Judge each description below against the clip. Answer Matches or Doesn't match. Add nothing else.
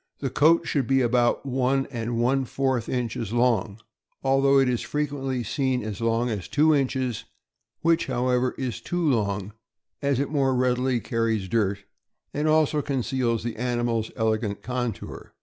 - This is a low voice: Matches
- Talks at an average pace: Matches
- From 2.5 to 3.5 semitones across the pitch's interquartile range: Matches